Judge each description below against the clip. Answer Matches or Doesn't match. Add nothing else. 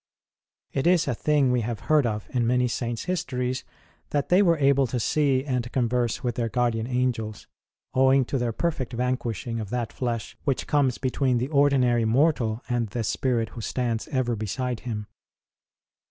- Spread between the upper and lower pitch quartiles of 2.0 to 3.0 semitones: Matches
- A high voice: Doesn't match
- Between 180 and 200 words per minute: Doesn't match